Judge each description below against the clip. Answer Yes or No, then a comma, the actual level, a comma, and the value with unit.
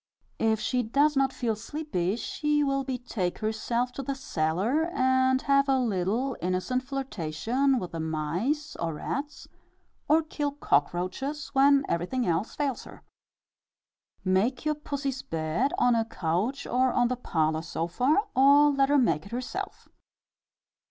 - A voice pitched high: Yes, very high, 250 Hz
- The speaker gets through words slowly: No, average, 145 wpm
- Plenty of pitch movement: Yes, wide, 7.0 semitones